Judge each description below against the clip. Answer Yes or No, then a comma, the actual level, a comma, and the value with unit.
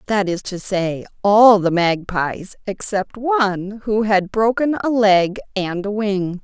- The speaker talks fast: No, average, 160 wpm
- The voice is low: No, high, 205 Hz